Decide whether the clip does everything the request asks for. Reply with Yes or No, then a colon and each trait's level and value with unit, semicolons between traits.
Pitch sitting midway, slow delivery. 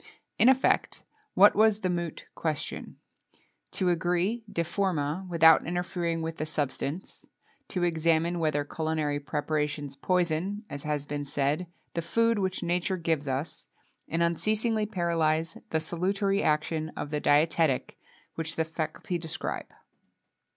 Yes: medium, 165 Hz; slow, 130 wpm